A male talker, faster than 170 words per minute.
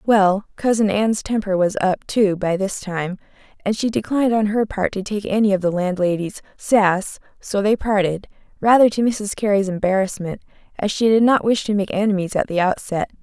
No: female; average, 190 wpm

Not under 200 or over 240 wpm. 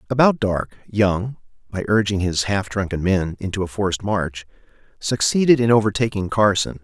No: average, 150 wpm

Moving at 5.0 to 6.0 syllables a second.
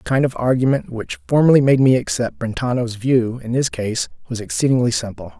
Yes: 5.7 syllables/s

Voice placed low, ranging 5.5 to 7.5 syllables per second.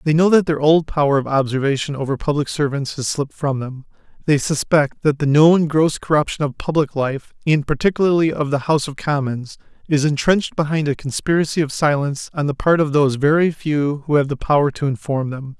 No: medium, 145 Hz; 5.7 syllables/s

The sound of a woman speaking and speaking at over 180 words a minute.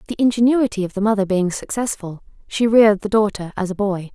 Yes: female; fast, 205 wpm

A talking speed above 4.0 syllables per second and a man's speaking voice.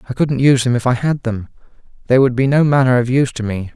Yes: 6.7 syllables/s; male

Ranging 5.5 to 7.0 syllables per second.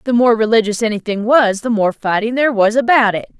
Yes: 6.0 syllables/s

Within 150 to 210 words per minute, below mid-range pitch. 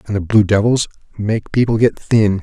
Yes: average, 200 wpm; low, 105 Hz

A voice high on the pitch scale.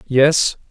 No: medium, 140 Hz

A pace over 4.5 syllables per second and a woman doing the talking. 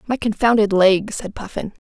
Yes: 4.9 syllables/s; female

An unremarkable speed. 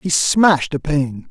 Yes: average, 185 wpm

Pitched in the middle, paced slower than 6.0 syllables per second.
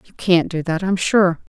Yes: medium, 180 Hz; 4.5 syllables/s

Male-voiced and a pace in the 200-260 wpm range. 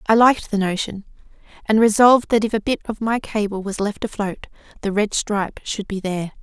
No: female; fast, 205 wpm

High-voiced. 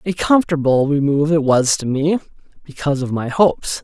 No: medium, 150 Hz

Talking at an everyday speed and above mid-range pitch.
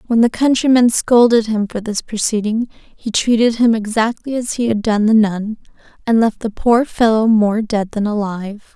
Yes: average, 185 wpm; high, 220 Hz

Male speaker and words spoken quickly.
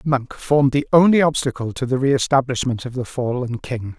No: male; average, 195 wpm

